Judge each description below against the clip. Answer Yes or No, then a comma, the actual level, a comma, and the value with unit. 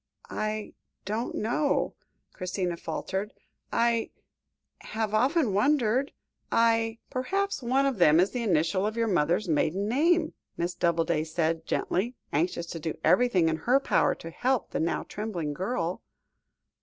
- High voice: Yes, high, 210 Hz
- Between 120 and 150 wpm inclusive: Yes, average, 145 wpm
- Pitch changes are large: Yes, wide, 6.2 semitones